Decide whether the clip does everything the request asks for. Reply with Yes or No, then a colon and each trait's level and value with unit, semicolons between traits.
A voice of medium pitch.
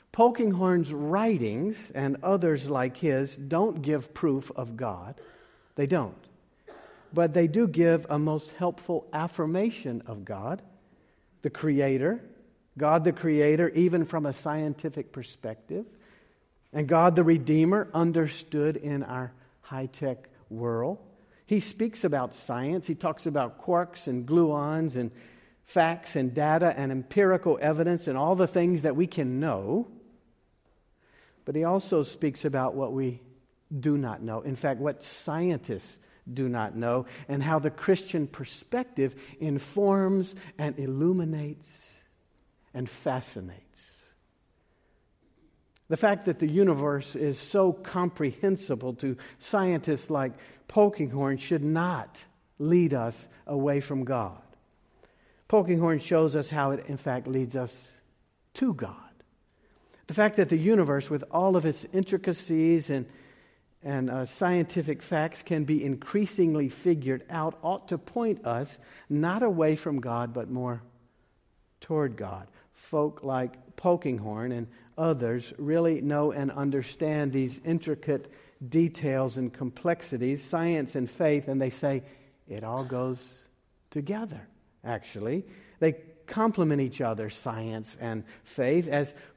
Yes: medium, 150 Hz